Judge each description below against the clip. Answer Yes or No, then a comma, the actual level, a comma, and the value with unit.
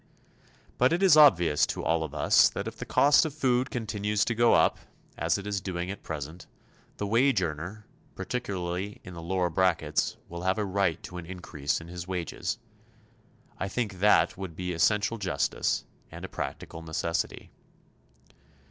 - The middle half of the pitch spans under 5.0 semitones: Yes, average, 3.9 semitones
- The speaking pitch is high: No, very low, 95 Hz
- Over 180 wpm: No, average, 170 wpm